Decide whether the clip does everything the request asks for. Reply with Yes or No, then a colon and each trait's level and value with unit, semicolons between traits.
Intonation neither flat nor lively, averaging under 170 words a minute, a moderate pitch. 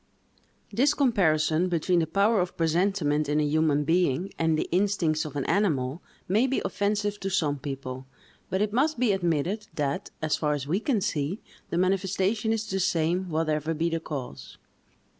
No: average, 4.8 semitones; average, 175 wpm; medium, 170 Hz